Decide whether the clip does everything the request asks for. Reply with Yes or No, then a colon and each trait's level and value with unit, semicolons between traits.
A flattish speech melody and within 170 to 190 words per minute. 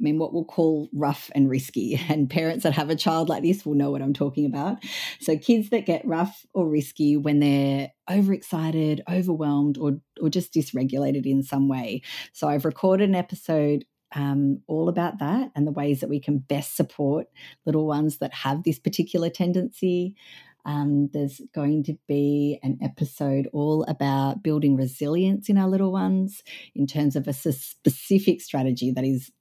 No: average, 3.2 semitones; average, 180 wpm